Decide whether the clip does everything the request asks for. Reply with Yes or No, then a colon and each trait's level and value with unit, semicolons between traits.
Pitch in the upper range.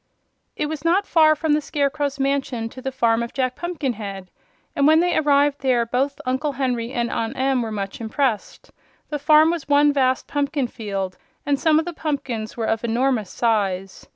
Yes: very high, 270 Hz